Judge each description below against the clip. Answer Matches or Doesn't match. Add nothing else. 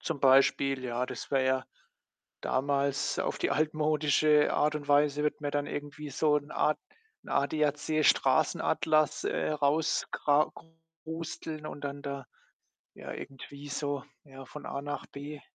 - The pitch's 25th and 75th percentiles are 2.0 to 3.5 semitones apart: Doesn't match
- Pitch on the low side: Doesn't match